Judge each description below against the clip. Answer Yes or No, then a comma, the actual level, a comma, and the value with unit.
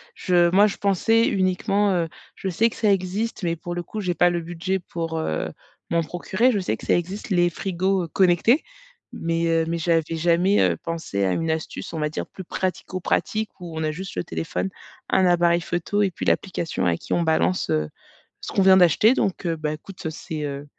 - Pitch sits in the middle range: Yes, medium, 175 Hz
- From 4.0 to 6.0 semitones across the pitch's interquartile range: No, average, 2.7 semitones